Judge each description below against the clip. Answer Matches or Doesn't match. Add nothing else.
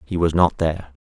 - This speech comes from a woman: Doesn't match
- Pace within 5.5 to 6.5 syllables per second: Matches